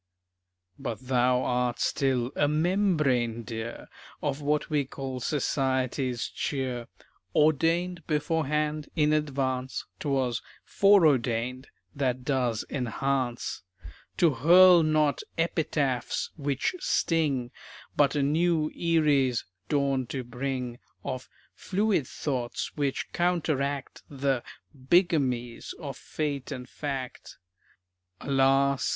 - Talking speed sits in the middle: No, slow, 95 wpm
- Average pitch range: Yes, average, 3.2 semitones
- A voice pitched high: No, medium, 140 Hz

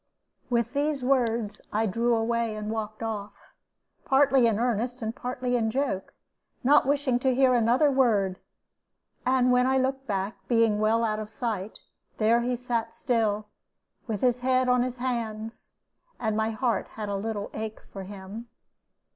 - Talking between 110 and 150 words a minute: No, average, 160 wpm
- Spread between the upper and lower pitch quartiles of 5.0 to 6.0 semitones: No, average, 2.7 semitones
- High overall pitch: Yes, high, 230 Hz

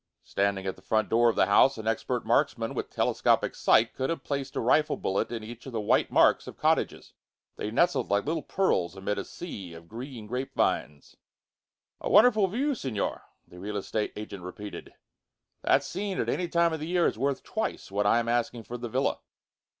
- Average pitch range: No, wide, 6.2 semitones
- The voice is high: No, low, 120 Hz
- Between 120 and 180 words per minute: No, fast, 205 wpm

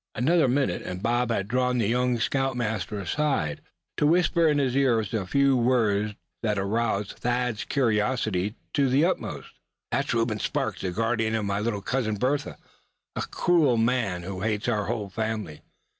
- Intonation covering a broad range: No, average, 3.6 semitones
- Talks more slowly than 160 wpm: No, average, 165 wpm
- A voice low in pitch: Yes, low, 115 Hz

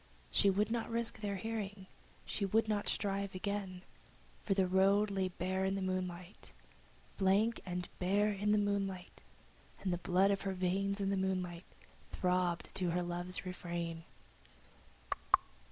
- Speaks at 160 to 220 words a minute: No, average, 150 wpm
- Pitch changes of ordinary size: No, narrow, 1.8 semitones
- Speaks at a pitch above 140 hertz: Yes, high, 190 Hz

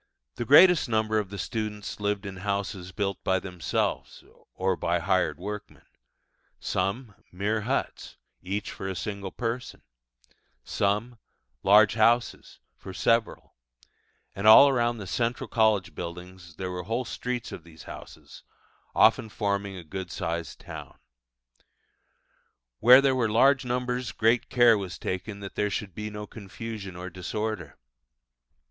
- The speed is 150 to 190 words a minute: No, average, 140 wpm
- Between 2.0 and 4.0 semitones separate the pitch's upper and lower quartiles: Yes, average, 3.5 semitones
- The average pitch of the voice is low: Yes, low, 105 Hz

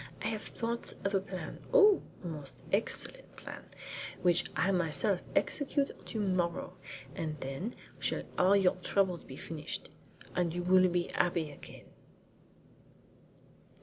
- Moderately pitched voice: Yes, medium, 180 Hz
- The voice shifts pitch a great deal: No, average, 2.9 semitones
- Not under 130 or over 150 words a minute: Yes, average, 140 wpm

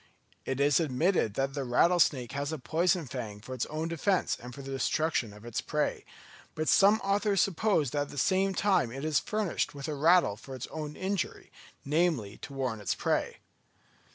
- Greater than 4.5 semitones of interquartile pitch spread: Yes, wide, 5.5 semitones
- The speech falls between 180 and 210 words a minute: Yes, average, 190 wpm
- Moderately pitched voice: Yes, medium, 145 Hz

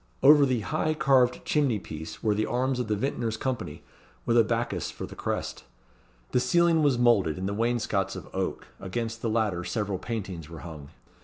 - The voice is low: Yes, low, 115 Hz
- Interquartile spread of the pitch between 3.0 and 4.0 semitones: No, average, 4.4 semitones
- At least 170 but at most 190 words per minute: Yes, average, 185 wpm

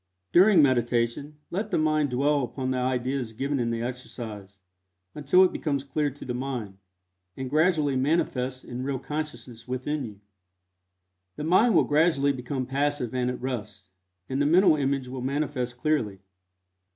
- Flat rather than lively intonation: No, average, 3.2 semitones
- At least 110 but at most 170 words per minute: Yes, average, 155 wpm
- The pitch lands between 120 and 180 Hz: Yes, low, 135 Hz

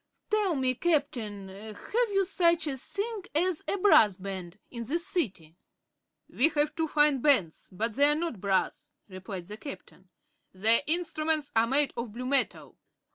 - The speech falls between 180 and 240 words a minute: No, average, 160 wpm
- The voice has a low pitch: No, very high, 270 Hz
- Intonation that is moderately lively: No, wide, 7.8 semitones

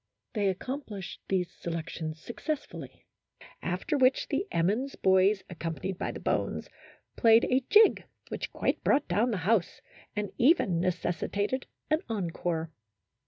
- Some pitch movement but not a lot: No, wide, 6.5 semitones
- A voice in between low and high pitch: No, high, 200 Hz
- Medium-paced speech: No, slow, 130 wpm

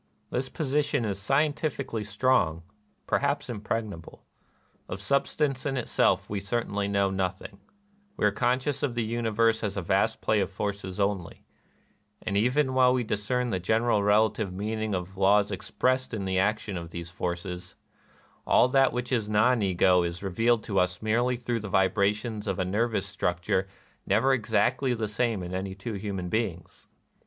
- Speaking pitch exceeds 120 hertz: No, low, 105 Hz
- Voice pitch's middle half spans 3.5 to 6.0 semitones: Yes, average, 4.0 semitones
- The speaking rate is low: No, average, 165 wpm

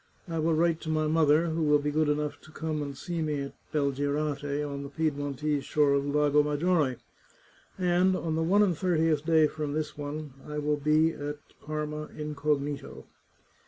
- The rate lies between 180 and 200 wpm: Yes, average, 185 wpm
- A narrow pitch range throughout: Yes, narrow, 1.6 semitones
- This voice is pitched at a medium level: Yes, medium, 150 Hz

